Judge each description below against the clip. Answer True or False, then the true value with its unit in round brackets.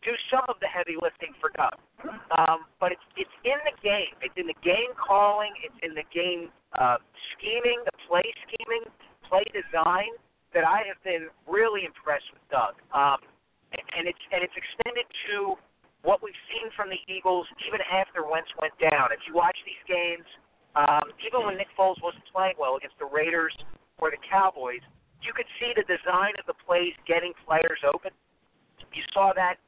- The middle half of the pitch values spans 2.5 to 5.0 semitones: False (5.6 semitones)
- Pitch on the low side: False (185 Hz)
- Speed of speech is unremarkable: True (185 wpm)